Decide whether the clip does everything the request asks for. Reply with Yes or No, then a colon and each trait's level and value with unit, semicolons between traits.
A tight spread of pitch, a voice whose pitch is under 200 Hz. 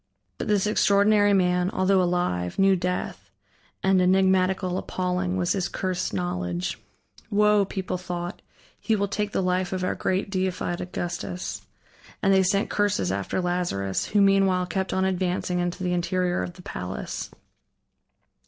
Yes: narrow, 1.5 semitones; medium, 185 Hz